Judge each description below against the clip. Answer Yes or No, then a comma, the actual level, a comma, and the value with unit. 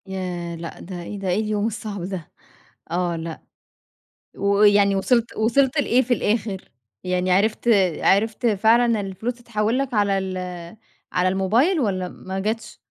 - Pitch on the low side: No, high, 205 Hz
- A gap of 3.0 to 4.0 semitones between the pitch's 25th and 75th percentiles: Yes, average, 3.4 semitones